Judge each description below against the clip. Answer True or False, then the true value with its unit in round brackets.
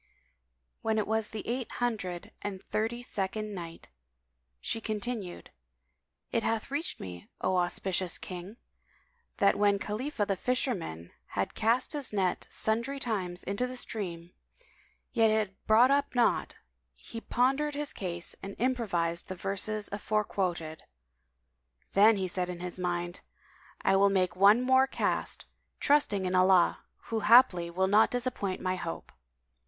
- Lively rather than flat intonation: False (4.4 semitones)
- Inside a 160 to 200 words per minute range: False (145 wpm)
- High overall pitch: True (205 Hz)